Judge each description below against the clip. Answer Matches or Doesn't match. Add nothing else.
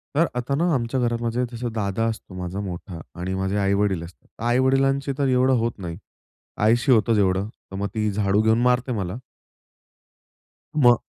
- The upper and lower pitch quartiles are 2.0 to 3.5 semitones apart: Doesn't match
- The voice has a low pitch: Matches